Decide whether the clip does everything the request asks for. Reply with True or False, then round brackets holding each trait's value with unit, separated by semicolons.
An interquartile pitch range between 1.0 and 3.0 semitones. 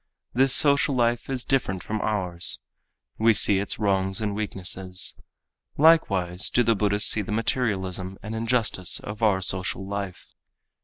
False (3.4 semitones)